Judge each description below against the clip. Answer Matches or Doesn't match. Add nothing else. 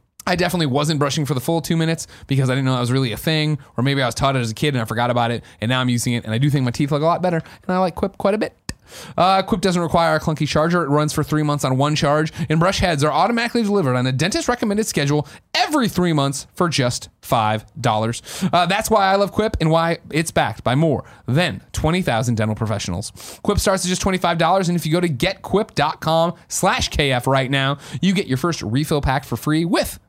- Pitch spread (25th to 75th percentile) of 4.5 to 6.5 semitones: Matches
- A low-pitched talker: Doesn't match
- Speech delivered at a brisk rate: Matches